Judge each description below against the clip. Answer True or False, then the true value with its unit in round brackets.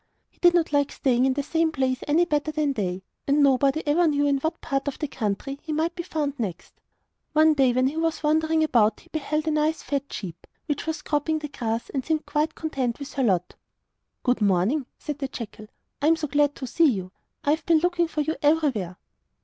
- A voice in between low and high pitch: False (290 Hz)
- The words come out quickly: True (220 wpm)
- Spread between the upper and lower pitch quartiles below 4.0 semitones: True (3.5 semitones)